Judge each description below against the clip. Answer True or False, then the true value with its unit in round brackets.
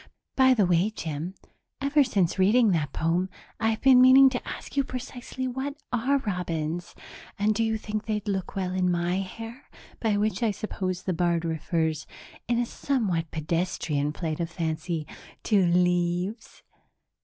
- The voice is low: False (190 Hz)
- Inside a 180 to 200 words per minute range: False (155 wpm)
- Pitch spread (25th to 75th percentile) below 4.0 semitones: False (5.1 semitones)